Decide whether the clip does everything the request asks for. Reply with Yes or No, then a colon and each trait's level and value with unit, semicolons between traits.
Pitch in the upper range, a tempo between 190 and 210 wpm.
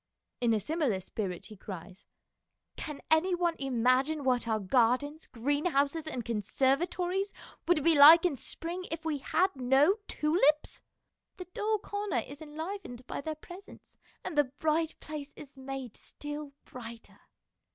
No: very high, 290 Hz; average, 145 wpm